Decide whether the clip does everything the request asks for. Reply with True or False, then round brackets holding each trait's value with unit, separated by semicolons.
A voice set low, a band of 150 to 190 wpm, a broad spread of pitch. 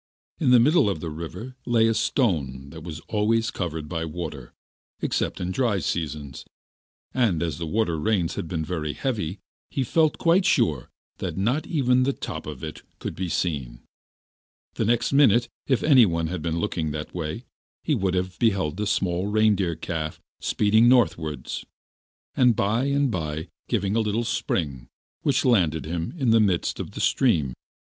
True (95 Hz; 170 wpm; 6.6 semitones)